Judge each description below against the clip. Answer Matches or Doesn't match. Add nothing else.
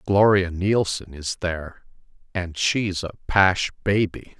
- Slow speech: Matches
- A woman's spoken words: Doesn't match